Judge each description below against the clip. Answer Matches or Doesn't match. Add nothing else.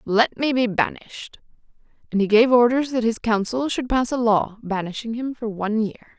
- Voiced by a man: Doesn't match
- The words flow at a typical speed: Matches